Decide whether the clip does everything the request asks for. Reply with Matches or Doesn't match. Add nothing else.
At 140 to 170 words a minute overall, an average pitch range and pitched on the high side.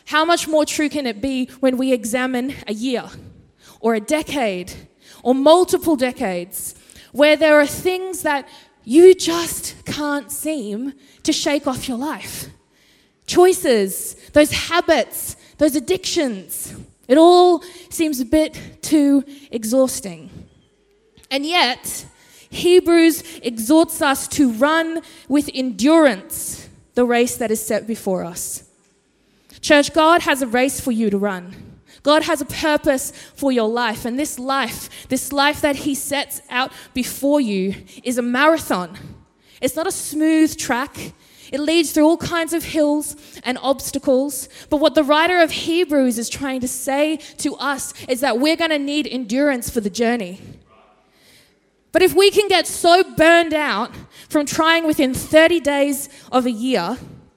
Matches